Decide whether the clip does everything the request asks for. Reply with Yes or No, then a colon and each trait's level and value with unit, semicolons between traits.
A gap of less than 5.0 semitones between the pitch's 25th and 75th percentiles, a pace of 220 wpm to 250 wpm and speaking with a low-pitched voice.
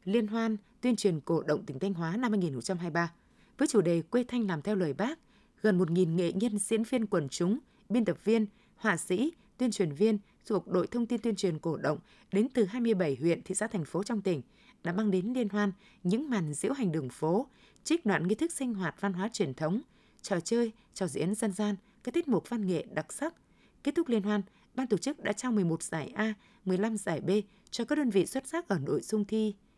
No: average, 4.1 semitones; average, 230 wpm; high, 205 Hz